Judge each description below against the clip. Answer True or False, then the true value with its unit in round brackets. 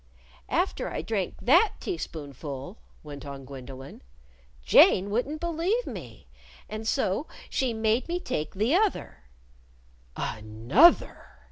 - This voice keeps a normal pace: False (105 wpm)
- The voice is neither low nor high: False (215 Hz)